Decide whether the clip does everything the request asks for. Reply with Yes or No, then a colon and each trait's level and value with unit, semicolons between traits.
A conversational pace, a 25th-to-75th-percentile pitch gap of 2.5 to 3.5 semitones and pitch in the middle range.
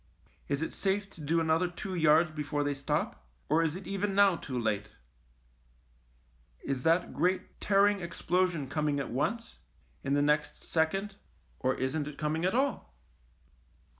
No: average, 160 wpm; average, 4.4 semitones; medium, 160 Hz